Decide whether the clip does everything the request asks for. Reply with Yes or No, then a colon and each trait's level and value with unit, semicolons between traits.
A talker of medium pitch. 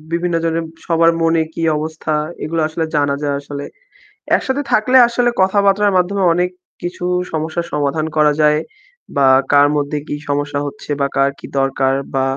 Yes: medium, 160 Hz